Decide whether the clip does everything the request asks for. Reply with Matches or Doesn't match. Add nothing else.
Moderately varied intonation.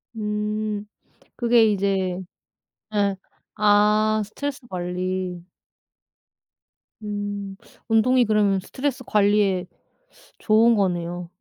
Doesn't match